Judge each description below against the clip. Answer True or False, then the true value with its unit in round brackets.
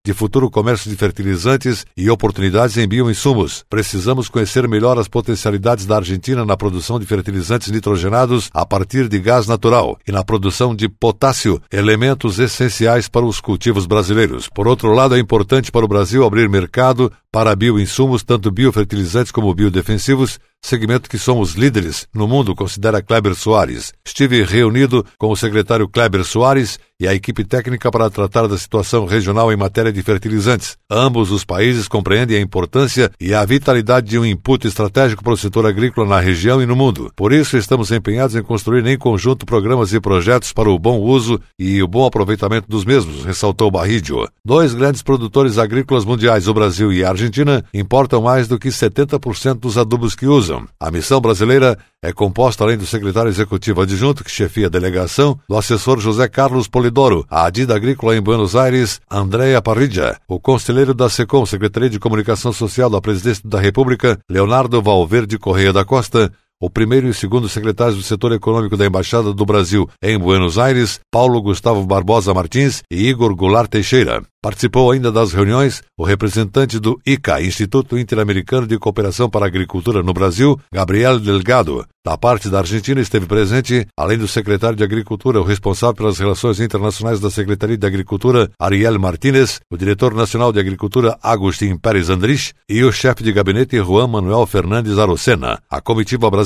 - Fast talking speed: False (170 wpm)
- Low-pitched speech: True (110 Hz)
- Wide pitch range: False (3.4 semitones)